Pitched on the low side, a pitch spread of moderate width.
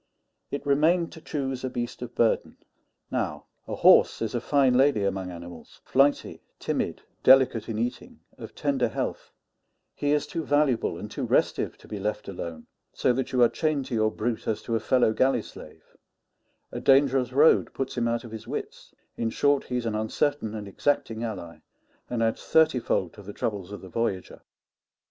Yes: low, 120 Hz; average, 4.0 semitones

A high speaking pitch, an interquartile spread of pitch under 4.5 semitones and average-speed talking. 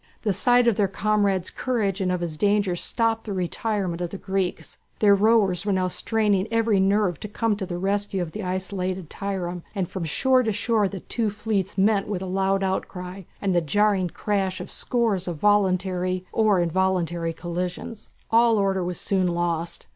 Yes: high, 195 Hz; narrow, 2.5 semitones; average, 180 wpm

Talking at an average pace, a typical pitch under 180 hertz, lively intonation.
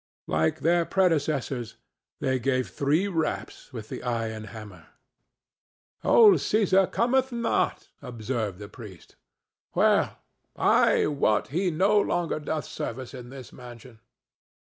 No: slow, 120 wpm; low, 135 Hz; wide, 7.3 semitones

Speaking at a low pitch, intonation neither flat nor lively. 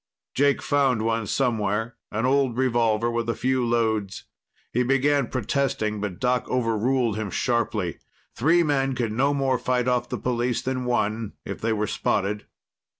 Yes: low, 120 Hz; average, 3.0 semitones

